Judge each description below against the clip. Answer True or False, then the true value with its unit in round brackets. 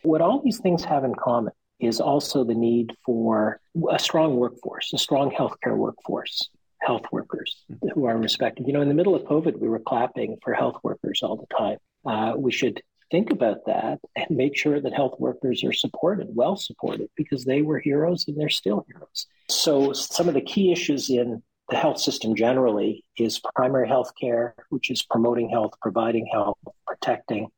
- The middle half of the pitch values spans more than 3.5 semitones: True (4.7 semitones)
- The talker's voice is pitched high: False (135 Hz)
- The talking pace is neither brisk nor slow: True (185 wpm)